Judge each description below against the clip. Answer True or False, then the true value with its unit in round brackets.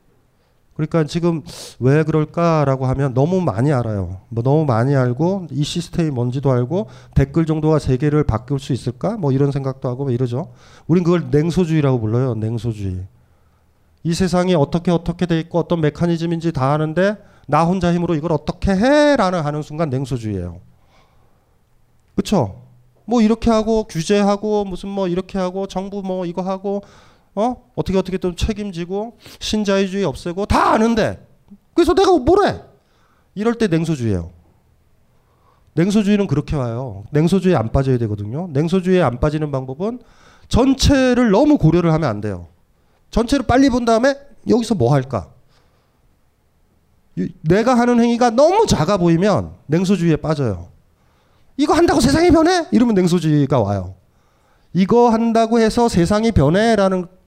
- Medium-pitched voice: True (170 Hz)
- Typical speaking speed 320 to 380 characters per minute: True (330 characters per minute)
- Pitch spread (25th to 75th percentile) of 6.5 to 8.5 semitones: True (7.4 semitones)